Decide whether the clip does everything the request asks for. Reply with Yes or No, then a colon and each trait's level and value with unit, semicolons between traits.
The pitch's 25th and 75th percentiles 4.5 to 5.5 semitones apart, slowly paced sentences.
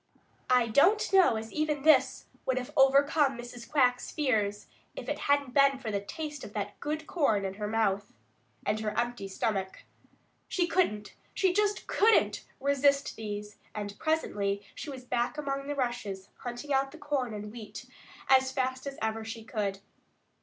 No: average, 5.1 semitones; average, 165 wpm